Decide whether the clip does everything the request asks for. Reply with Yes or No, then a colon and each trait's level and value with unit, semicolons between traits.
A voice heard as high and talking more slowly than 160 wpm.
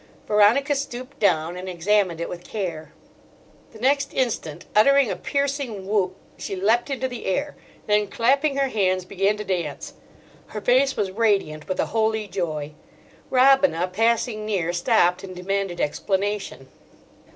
Yes: high, 210 Hz; average, 145 wpm